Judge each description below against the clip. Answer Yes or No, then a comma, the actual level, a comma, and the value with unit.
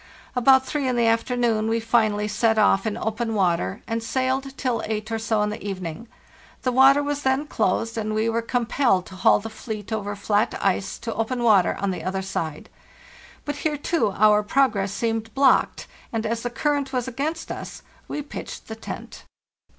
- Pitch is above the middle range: Yes, high, 225 Hz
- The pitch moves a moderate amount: Yes, average, 3.6 semitones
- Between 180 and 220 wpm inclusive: Yes, average, 190 wpm